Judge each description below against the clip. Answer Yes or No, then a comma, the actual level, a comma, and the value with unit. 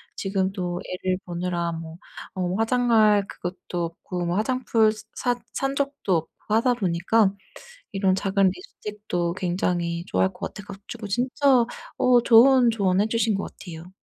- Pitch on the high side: Yes, high, 195 Hz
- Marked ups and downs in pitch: No, average, 4.5 semitones